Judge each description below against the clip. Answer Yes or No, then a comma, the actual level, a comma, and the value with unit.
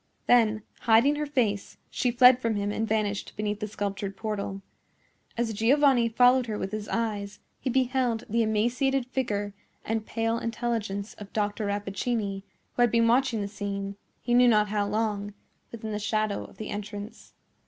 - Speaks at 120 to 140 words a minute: No, average, 165 wpm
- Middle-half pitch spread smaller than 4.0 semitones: Yes, average, 2.7 semitones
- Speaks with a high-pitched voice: Yes, high, 220 Hz